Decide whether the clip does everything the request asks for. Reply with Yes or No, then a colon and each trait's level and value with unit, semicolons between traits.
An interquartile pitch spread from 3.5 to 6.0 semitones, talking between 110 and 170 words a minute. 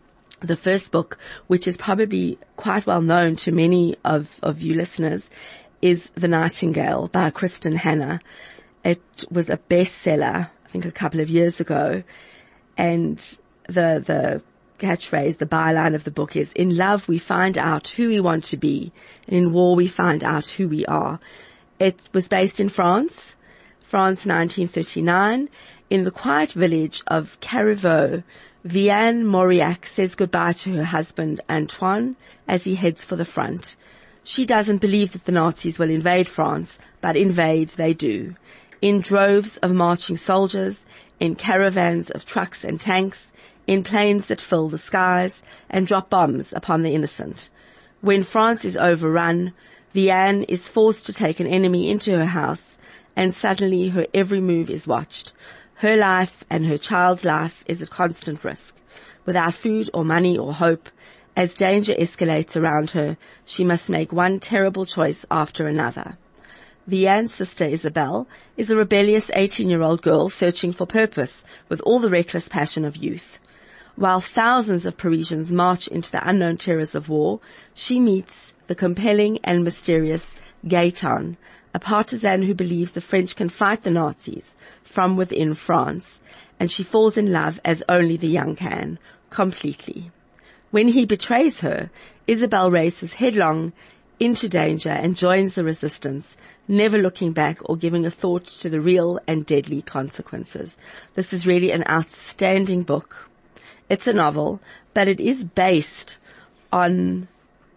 No: average, 2.8 semitones; average, 155 wpm